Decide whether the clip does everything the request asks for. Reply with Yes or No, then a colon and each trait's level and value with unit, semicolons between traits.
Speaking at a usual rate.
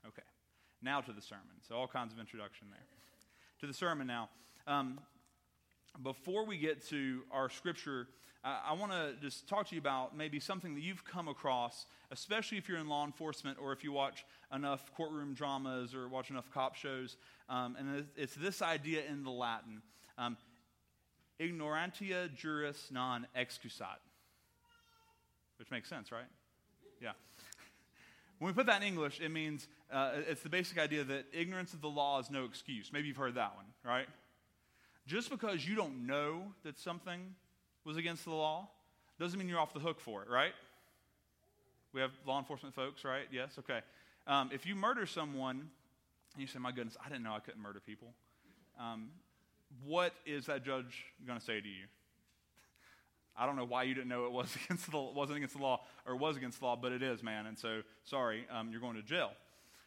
Yes: average, 190 wpm